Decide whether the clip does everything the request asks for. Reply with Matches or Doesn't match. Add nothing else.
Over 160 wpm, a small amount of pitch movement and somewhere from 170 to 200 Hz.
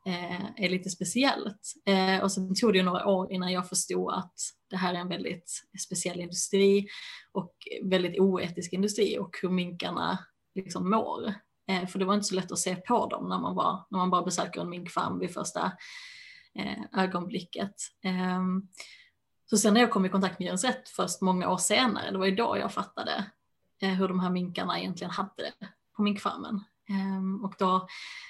Matches